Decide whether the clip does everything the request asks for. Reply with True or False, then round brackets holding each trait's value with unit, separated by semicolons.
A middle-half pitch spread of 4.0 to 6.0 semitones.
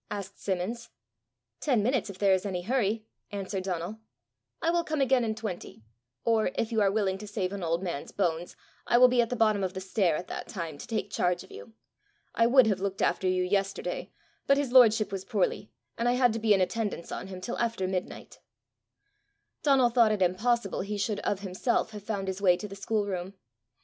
False (3.6 semitones)